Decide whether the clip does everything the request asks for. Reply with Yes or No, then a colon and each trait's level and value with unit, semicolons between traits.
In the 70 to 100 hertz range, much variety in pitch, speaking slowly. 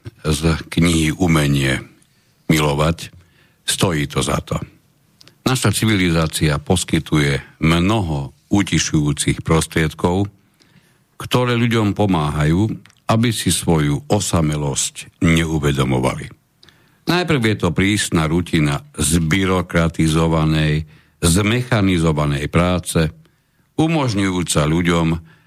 Yes: very low, 85 Hz; wide, 5.7 semitones; slow, 75 wpm